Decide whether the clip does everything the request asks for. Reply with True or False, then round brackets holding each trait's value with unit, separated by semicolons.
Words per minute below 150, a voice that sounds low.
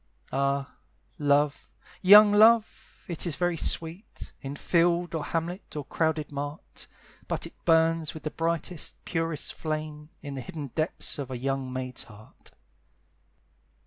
False (140 wpm; 155 Hz)